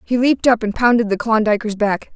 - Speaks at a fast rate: Yes, fast, 220 wpm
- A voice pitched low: No, high, 225 Hz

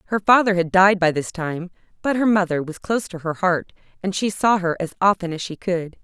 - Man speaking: No, female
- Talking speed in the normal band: No, fast, 240 wpm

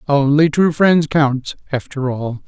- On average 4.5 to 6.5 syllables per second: No, 3.8 syllables/s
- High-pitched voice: No, medium, 145 Hz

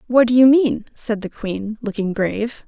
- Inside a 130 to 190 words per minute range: No, average, 200 wpm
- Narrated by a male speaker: No, female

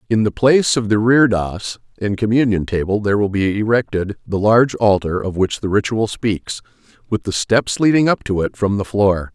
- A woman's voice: No, male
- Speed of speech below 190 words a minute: No, average, 200 wpm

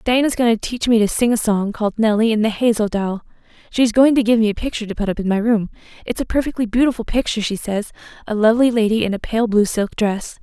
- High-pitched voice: Yes, high, 220 Hz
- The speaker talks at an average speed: No, fast, 255 wpm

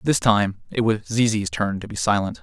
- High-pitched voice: No, low, 110 Hz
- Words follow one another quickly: Yes, fast, 225 wpm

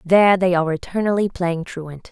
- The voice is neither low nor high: Yes, medium, 180 Hz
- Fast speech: No, average, 170 wpm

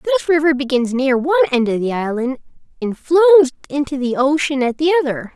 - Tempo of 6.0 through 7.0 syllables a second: Yes, 6.7 syllables/s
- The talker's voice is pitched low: No, very high, 280 Hz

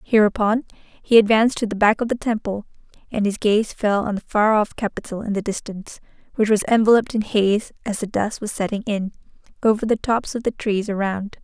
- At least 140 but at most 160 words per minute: No, fast, 205 wpm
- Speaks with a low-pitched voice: No, high, 215 Hz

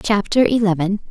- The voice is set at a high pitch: Yes, high, 205 Hz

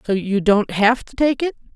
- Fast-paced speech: Yes, fast, 240 wpm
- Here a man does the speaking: No, female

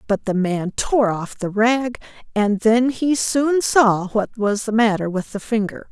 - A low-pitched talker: No, high, 220 Hz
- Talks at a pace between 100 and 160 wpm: No, average, 195 wpm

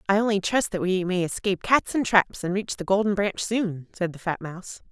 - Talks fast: Yes, fast, 245 wpm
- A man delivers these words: No, female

